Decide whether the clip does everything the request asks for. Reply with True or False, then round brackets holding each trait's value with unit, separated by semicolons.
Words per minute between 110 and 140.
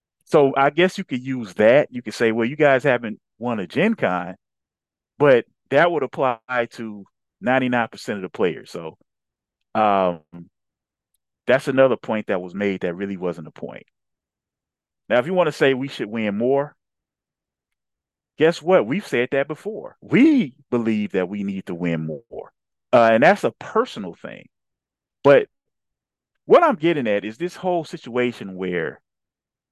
False (160 wpm)